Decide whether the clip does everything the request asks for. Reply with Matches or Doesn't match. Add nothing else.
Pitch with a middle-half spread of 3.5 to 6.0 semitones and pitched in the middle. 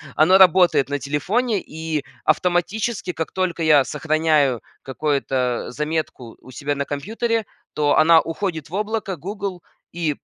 Matches